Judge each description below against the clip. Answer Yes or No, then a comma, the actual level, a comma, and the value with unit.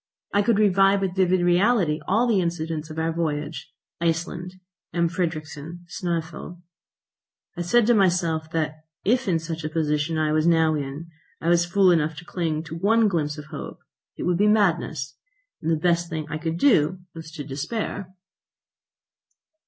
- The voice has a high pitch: No, medium, 170 Hz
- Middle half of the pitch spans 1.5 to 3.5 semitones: Yes, average, 2.9 semitones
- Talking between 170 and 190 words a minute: Yes, average, 175 wpm